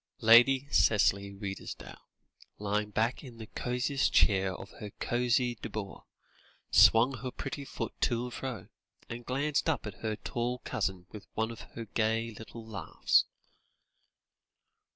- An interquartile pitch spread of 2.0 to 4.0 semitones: Yes, average, 2.8 semitones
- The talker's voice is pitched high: No, low, 115 Hz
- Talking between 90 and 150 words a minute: Yes, slow, 135 wpm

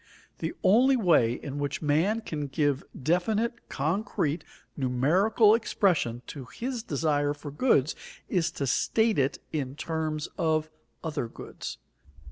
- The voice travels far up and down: Yes, wide, 6.3 semitones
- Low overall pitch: No, medium, 155 Hz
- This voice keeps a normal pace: No, slow, 125 wpm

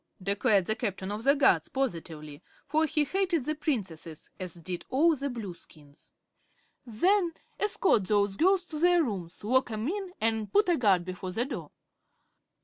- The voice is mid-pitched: No, high, 230 Hz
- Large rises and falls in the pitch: Yes, wide, 8.7 semitones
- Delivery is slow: No, average, 160 wpm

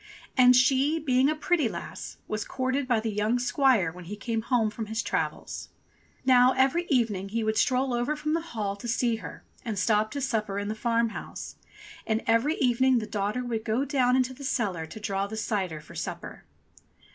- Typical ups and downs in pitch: Yes, average, 3.4 semitones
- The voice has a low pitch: No, high, 235 Hz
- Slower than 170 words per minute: No, average, 200 wpm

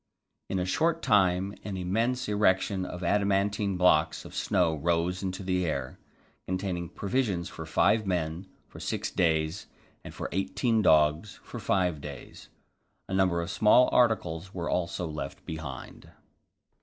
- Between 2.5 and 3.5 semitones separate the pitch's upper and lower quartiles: Yes, average, 3.1 semitones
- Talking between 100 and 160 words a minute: Yes, average, 145 wpm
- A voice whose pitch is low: Yes, very low, 90 Hz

